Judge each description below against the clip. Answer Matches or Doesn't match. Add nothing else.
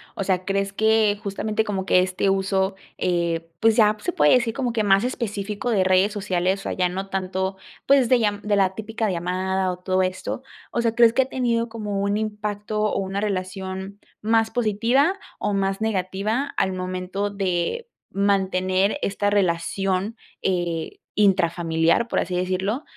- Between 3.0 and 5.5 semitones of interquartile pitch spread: Doesn't match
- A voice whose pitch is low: Doesn't match